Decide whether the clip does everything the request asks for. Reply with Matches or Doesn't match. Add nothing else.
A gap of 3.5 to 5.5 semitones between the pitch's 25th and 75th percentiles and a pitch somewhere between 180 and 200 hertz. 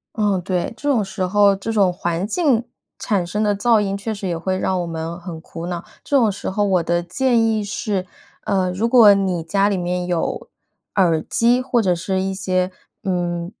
Doesn't match